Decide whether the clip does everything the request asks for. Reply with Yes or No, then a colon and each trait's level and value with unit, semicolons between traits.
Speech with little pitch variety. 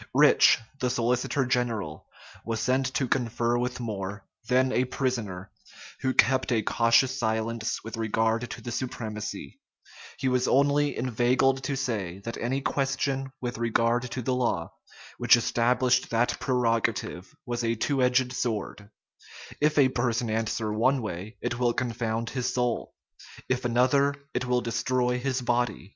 Yes: narrow, 2.1 semitones